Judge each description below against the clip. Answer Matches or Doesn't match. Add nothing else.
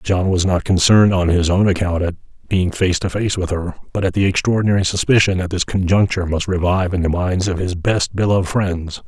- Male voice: Matches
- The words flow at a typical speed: Doesn't match